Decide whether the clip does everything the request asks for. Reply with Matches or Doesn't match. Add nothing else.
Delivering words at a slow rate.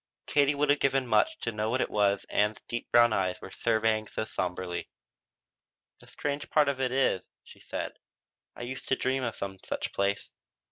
Doesn't match